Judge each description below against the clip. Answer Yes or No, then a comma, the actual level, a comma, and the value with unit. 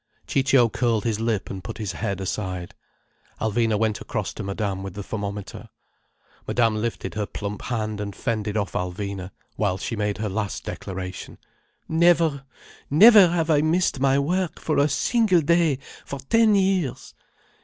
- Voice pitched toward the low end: Yes, low, 115 Hz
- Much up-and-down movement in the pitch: Yes, wide, 6.7 semitones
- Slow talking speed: No, average, 155 wpm